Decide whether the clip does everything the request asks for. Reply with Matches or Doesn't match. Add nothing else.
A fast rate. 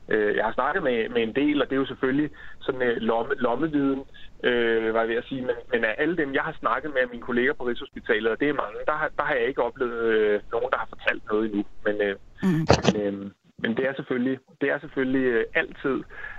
Matches